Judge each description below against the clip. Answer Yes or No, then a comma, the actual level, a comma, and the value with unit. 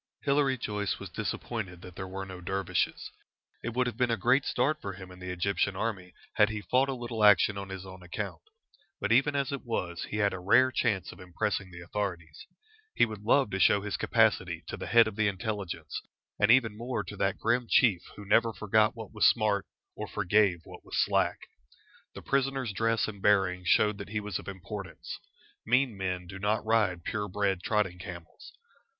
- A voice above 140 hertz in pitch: No, low, 105 Hz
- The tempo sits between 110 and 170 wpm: No, average, 200 wpm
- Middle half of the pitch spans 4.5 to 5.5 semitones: No, average, 3.3 semitones